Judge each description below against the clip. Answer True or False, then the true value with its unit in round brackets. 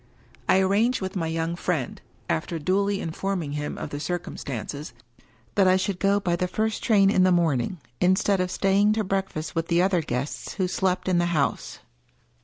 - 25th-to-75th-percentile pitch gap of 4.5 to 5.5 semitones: False (3.2 semitones)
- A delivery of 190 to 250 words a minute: True (200 wpm)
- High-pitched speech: False (180 Hz)